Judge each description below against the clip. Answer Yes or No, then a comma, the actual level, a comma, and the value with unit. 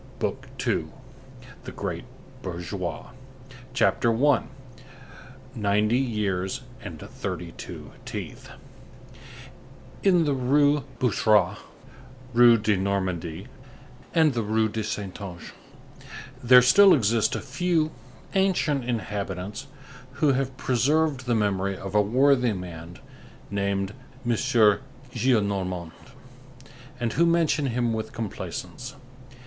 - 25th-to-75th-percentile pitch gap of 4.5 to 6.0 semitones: Yes, average, 5.1 semitones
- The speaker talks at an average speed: No, slow, 100 wpm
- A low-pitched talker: Yes, low, 115 Hz